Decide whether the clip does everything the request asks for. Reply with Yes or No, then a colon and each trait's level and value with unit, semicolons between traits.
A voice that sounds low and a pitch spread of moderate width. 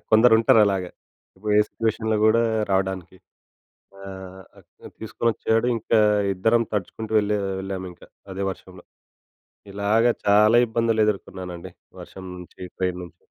Yes: low, 105 Hz; average, 3.1 semitones